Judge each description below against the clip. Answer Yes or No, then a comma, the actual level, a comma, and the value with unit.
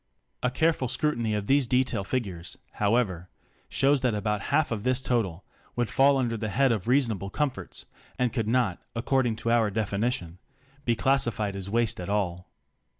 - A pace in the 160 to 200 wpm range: Yes, average, 165 wpm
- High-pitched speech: No, low, 115 Hz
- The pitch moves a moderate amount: Yes, average, 4.0 semitones